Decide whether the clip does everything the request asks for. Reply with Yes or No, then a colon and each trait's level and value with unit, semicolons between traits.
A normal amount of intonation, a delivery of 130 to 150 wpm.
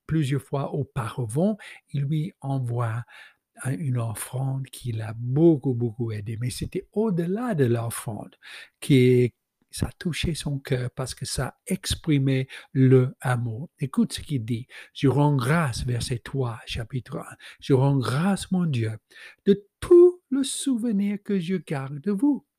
No: wide, 6.2 semitones; slow, 145 wpm